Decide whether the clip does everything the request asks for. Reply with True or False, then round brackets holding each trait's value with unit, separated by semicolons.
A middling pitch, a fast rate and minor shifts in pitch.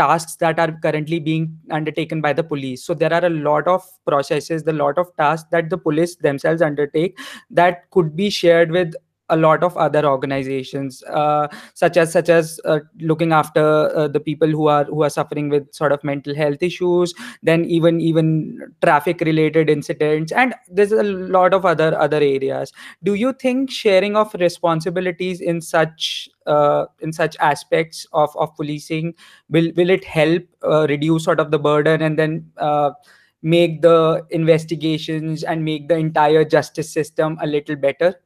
False (160 Hz; 175 wpm; 2.1 semitones)